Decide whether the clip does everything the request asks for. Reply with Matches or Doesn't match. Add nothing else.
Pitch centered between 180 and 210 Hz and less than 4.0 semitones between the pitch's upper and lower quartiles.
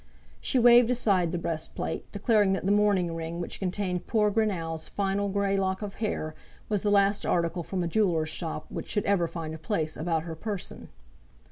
Matches